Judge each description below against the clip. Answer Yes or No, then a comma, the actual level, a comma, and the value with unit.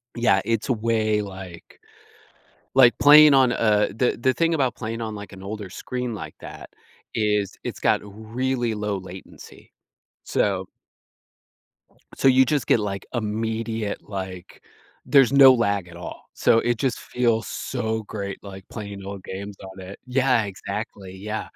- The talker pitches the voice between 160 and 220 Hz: No, low, 110 Hz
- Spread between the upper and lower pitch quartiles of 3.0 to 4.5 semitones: Yes, average, 3.5 semitones